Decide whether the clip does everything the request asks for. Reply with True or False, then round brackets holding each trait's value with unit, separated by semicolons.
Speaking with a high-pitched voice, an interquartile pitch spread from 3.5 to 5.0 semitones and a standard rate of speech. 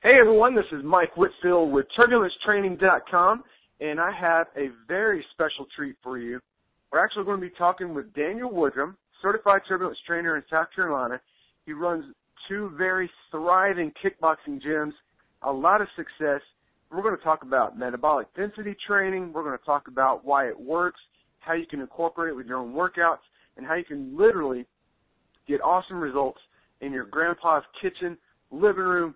False (165 Hz; 4.5 semitones; 170 wpm)